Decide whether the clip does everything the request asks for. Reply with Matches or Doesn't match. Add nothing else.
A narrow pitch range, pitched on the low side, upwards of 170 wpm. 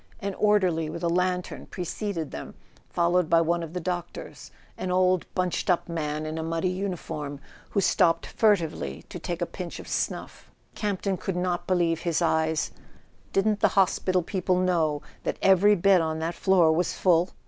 Doesn't match